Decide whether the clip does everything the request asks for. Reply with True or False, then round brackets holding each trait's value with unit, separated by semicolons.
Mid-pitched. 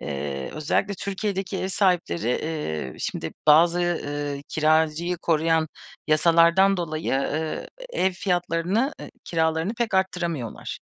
True (165 Hz)